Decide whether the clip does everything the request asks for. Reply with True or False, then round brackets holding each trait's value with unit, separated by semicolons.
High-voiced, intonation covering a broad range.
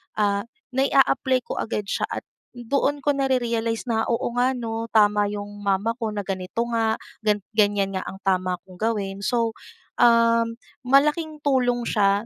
False (225 Hz; 3.3 semitones)